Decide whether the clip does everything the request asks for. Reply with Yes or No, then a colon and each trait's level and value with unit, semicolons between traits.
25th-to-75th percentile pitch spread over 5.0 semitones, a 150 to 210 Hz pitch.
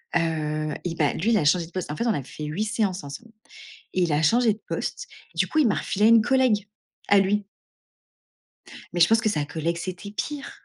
Yes: wide, 5.4 semitones; medium, 185 Hz